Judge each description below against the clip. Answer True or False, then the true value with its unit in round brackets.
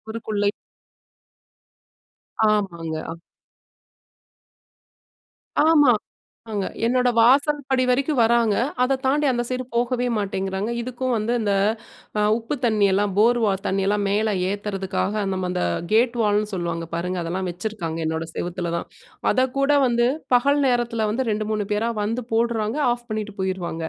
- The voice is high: True (215 Hz)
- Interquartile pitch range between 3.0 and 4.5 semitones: True (3.9 semitones)